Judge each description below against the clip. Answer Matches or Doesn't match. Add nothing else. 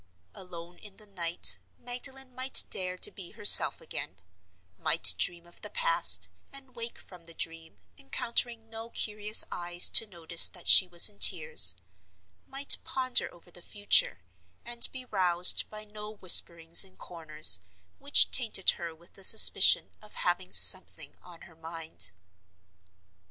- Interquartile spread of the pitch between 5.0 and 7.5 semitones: Matches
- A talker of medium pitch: Matches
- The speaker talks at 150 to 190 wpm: Doesn't match